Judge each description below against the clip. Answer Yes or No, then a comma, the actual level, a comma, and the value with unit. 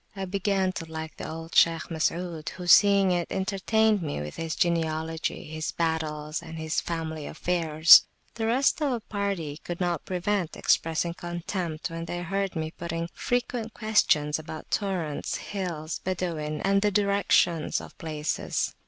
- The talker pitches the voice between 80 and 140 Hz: No, medium, 170 Hz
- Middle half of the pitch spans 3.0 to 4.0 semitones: Yes, average, 3.6 semitones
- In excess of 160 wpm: No, average, 155 wpm